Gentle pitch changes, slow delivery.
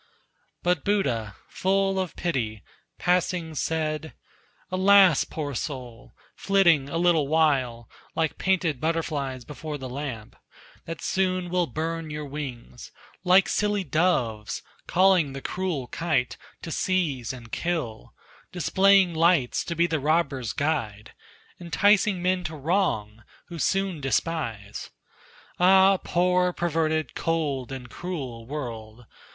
No: average, 5.3 semitones; slow, 120 wpm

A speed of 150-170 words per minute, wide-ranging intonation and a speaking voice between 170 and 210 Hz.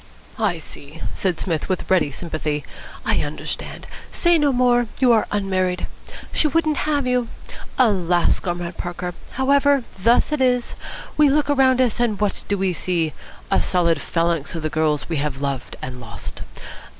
Yes: average, 160 wpm; wide, 7.5 semitones; medium, 185 Hz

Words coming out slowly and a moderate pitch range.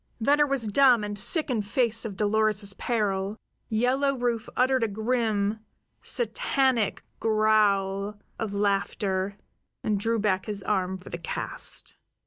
Yes: slow, 130 wpm; average, 3.2 semitones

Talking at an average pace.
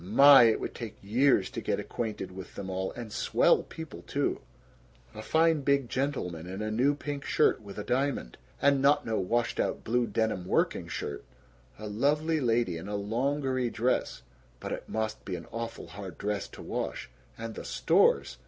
Yes: average, 180 wpm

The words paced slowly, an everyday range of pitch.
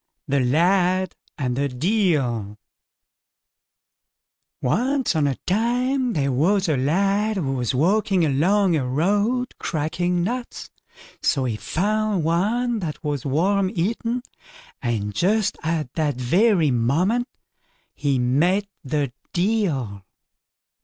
No: slow, 110 wpm; wide, 7.1 semitones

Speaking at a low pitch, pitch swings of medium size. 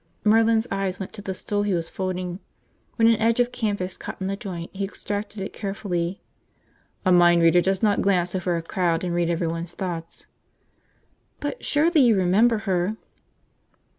No: high, 190 Hz; average, 3.2 semitones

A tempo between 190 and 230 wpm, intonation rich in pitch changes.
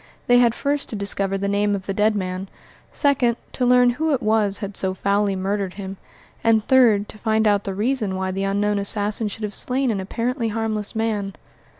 No: fast, 205 wpm; narrow, 2.6 semitones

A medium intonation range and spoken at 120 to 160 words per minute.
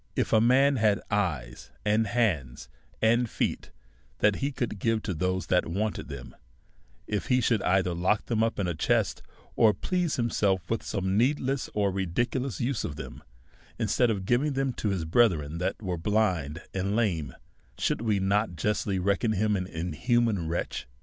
No: average, 4.5 semitones; average, 170 wpm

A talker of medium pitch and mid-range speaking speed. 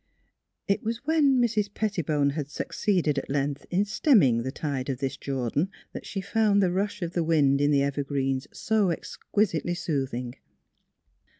Yes: medium, 155 Hz; average, 165 wpm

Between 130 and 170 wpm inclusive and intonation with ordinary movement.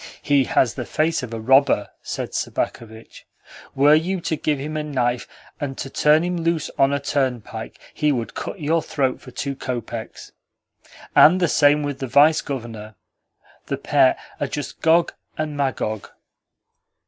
Yes: average, 160 wpm; average, 3.8 semitones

